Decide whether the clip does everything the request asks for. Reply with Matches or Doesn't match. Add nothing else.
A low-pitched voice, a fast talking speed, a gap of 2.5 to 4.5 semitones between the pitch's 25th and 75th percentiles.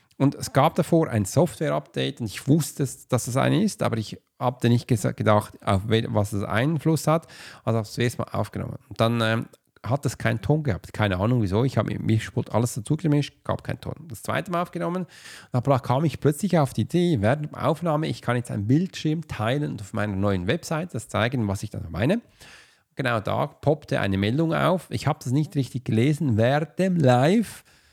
Doesn't match